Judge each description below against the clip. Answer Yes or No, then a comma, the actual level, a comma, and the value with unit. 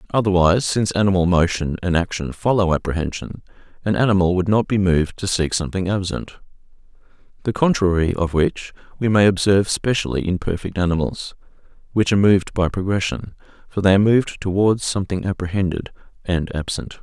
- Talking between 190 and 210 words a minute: No, average, 150 wpm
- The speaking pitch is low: Yes, very low, 95 Hz